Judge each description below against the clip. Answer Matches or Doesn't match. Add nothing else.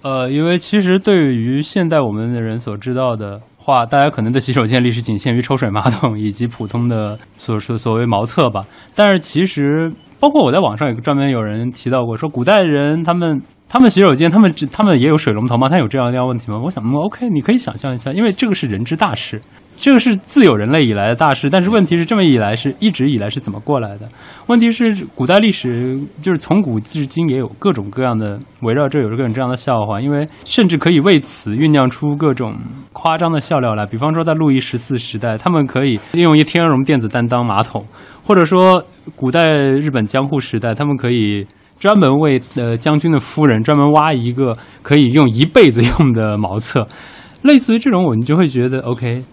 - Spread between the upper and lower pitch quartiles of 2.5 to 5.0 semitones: Doesn't match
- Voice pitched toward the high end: Doesn't match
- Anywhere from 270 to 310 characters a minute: Doesn't match